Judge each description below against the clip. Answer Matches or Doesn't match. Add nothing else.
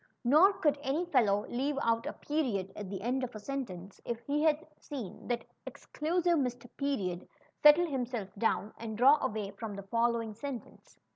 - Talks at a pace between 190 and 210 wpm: Doesn't match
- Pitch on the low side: Doesn't match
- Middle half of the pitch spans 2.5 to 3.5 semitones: Doesn't match